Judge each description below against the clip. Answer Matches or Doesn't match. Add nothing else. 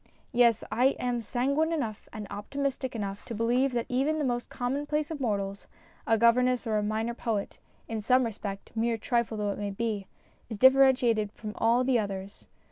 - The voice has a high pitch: Matches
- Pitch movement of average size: Matches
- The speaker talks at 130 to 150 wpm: Doesn't match